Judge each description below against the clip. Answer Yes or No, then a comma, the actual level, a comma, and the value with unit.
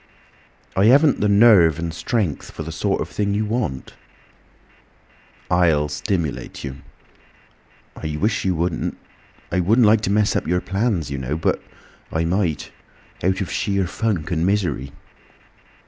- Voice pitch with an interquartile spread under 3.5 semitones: No, average, 4.4 semitones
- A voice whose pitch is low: Yes, very low, 90 Hz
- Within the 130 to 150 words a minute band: Yes, average, 145 wpm